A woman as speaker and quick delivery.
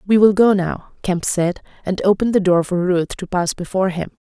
Yes: female; fast, 225 wpm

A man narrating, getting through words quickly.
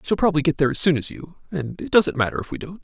Yes: male; fast, 340 wpm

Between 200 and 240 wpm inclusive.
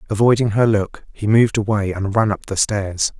Yes: fast, 205 wpm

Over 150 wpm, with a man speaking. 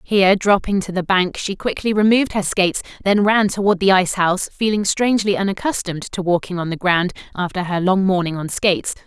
No: average, 200 wpm; female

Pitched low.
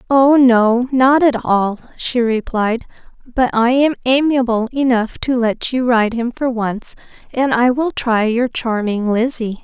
No: high, 240 Hz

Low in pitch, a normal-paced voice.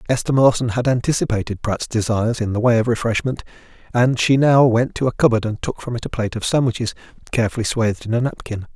No: low, 115 Hz; fast, 210 wpm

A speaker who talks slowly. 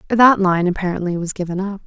No: average, 195 wpm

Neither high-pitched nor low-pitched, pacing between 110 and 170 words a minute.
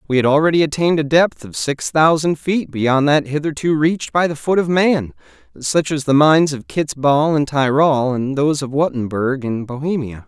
No: medium, 145 Hz; average, 200 wpm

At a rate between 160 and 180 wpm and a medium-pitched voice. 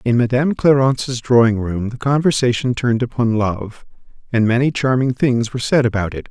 No: average, 170 wpm; low, 120 Hz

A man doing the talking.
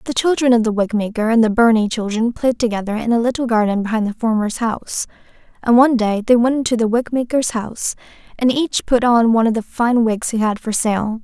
No: female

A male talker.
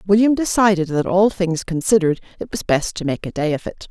No: female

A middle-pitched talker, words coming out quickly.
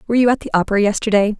No: high, 215 Hz; fast, 260 wpm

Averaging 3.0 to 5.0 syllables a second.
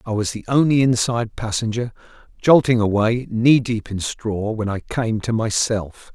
Yes: 4.5 syllables/s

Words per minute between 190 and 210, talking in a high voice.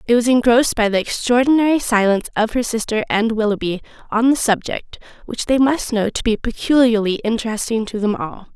No: average, 180 wpm; high, 230 Hz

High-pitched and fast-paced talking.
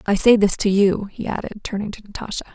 Yes: high, 205 Hz; fast, 235 wpm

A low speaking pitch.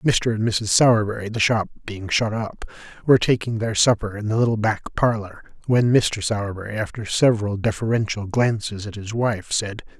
Yes: low, 110 Hz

